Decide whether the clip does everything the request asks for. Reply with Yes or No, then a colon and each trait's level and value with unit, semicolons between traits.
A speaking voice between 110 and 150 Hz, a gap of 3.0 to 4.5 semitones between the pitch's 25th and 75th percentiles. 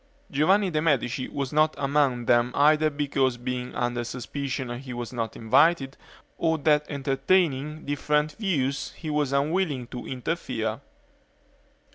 Yes: medium, 140 Hz; average, 3.4 semitones